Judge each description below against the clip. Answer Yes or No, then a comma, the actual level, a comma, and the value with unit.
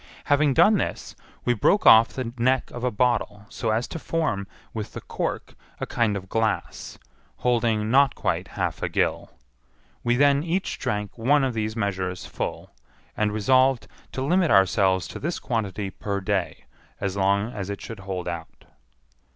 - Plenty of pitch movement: No, average, 4.5 semitones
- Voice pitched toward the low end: Yes, low, 110 Hz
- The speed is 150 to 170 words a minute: Yes, average, 165 wpm